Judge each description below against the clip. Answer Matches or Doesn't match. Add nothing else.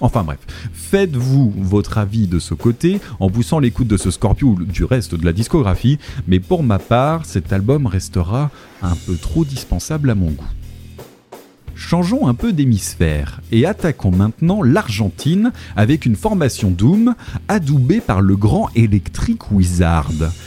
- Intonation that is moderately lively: Doesn't match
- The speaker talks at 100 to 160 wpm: Matches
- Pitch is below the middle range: Matches